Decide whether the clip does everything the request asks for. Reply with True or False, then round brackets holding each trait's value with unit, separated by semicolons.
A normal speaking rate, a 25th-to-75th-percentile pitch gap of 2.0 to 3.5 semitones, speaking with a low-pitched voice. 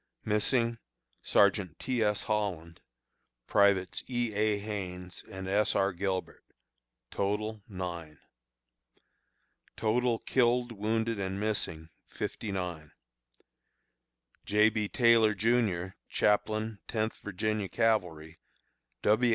False (95 wpm; 2.8 semitones; 105 Hz)